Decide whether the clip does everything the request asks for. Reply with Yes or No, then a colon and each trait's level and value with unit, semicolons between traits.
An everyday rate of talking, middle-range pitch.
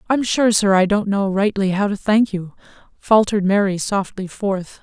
No: average, 185 wpm; high, 200 Hz